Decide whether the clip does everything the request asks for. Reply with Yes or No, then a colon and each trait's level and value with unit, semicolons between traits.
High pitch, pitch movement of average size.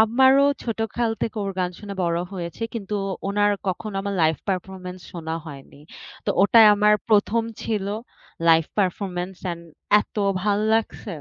Yes: high, 200 Hz; average, 3.4 semitones